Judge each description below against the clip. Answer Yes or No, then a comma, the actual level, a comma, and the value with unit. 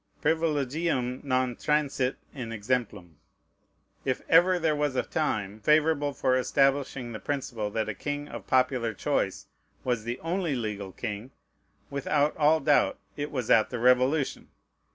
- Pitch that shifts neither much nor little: Yes, average, 4.0 semitones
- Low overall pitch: Yes, low, 130 Hz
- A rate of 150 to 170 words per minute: No, average, 140 wpm